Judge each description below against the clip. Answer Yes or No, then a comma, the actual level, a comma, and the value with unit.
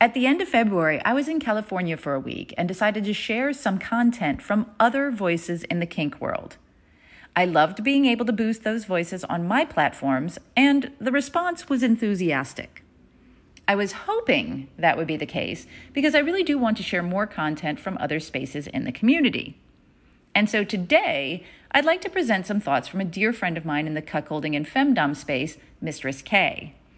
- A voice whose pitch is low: No, high, 205 Hz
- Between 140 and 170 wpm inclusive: No, average, 195 wpm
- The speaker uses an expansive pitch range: Yes, wide, 8.6 semitones